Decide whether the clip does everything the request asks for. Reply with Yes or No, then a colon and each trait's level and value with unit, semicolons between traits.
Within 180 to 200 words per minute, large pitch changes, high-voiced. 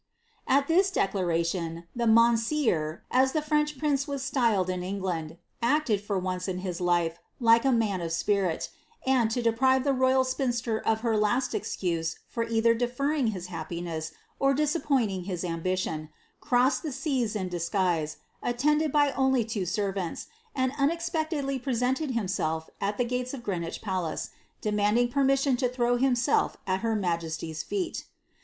No: average, 155 wpm; wide, 6.4 semitones; high, 230 Hz